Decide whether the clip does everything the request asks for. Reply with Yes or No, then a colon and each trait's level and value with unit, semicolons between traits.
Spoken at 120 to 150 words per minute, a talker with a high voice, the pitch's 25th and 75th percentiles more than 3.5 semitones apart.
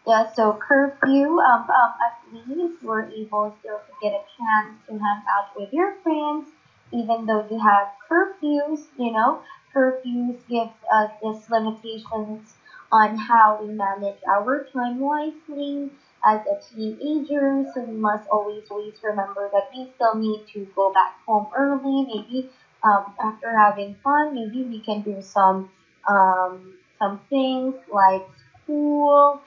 Yes: average, 145 wpm; high, 225 Hz; average, 4.5 semitones